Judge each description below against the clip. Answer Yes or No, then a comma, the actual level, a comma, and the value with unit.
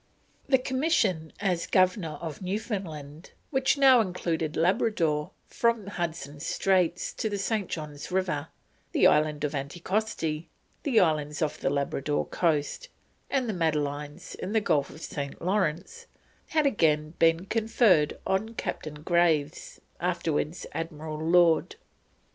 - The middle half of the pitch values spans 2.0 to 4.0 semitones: No, average, 5.2 semitones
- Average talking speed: No, slow, 125 wpm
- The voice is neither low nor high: Yes, medium, 170 Hz